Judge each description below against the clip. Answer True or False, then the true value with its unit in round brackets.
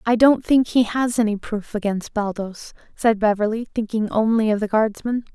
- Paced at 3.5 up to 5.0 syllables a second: True (4.9 syllables/s)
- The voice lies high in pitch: True (220 Hz)